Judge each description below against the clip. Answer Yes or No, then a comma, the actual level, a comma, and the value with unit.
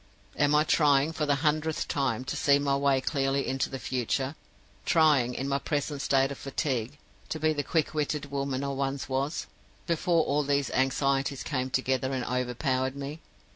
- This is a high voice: No, medium, 140 Hz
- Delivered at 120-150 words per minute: No, average, 175 wpm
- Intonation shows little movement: Yes, narrow, 1.8 semitones